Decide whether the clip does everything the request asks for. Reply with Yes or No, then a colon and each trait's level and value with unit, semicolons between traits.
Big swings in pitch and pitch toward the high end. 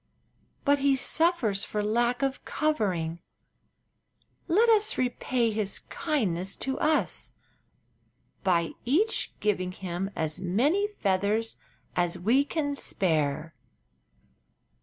Yes: wide, 7.7 semitones; high, 220 Hz